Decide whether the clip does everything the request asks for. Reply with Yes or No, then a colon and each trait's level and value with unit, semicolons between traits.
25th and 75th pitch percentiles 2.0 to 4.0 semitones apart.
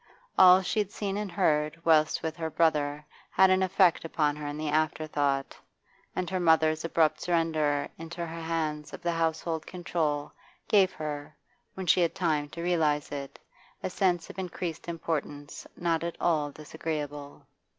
Yes: narrow, 2.5 semitones